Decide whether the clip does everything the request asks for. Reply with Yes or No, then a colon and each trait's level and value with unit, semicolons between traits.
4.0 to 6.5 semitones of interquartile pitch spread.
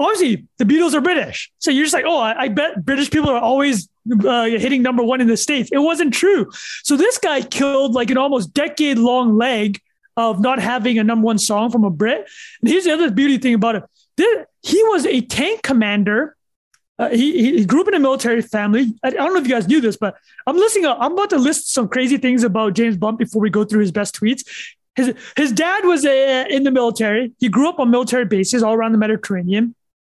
Yes: average, 4.8 semitones